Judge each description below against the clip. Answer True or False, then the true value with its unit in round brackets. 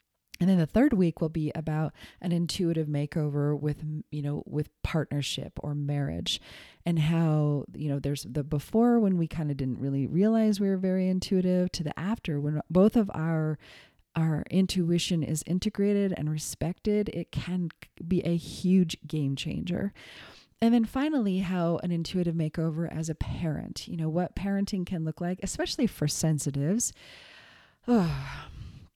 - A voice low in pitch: False (165 Hz)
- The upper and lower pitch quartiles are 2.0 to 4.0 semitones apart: True (3.7 semitones)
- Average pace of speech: True (160 wpm)